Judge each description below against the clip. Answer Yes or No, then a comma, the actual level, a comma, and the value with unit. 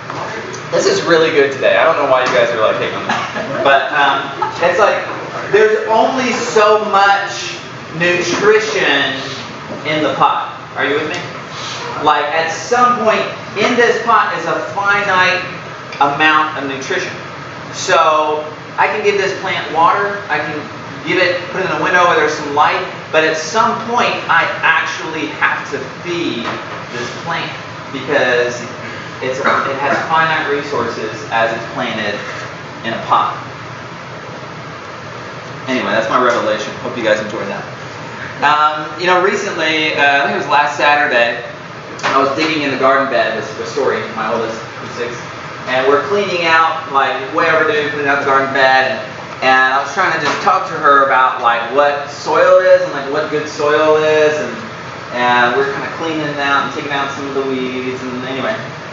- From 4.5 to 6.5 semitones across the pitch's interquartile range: Yes, average, 4.8 semitones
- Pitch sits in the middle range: Yes, medium, 155 Hz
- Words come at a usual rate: Yes, average, 175 wpm